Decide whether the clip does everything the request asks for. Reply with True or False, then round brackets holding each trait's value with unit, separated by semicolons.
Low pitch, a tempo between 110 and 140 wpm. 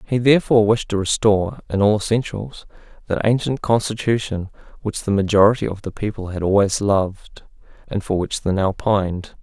False (105 Hz; 165 wpm)